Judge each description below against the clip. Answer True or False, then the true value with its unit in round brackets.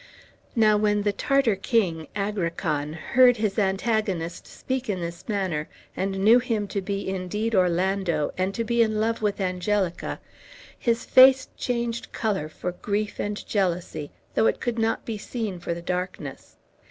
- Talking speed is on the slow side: False (155 wpm)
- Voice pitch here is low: False (205 Hz)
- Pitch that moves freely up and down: False (3.8 semitones)